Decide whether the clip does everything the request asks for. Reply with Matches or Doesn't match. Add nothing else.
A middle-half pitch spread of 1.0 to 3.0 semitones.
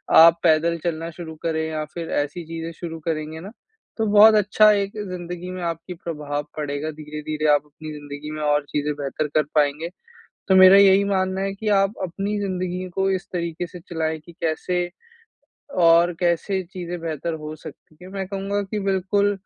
Doesn't match